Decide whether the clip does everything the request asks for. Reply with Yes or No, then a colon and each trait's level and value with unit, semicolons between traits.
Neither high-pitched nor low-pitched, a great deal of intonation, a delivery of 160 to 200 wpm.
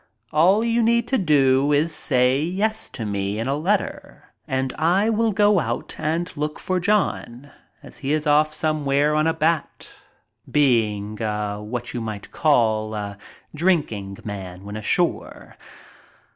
No: medium, 145 Hz; wide, 7.4 semitones; average, 145 wpm